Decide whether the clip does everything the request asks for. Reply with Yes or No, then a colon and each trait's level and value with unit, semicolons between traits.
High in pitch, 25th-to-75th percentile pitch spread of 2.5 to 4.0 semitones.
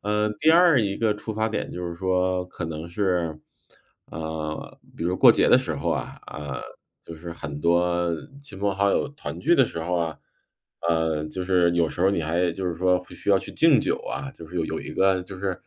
No: very low, 90 Hz; average, 3.2 semitones